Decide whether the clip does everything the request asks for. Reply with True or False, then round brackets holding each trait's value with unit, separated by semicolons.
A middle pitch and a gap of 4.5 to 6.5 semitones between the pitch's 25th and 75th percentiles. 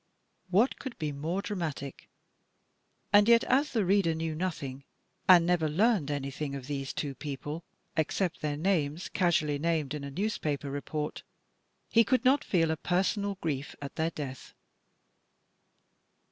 True (160 Hz; 5.0 semitones)